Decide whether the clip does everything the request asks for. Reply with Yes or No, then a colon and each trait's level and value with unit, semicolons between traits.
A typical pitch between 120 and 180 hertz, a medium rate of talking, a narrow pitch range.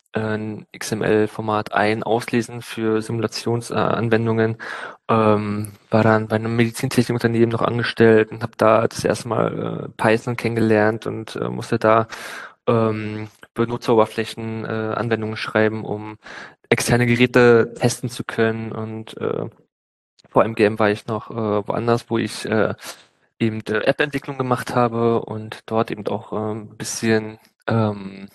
No: low, 110 Hz; average, 135 wpm; narrow, 1.3 semitones